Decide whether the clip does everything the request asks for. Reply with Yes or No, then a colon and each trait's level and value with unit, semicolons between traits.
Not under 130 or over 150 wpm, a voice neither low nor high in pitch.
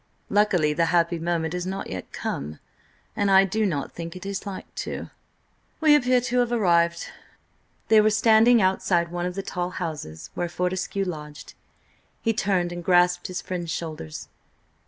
No: average, 160 wpm; medium, 180 Hz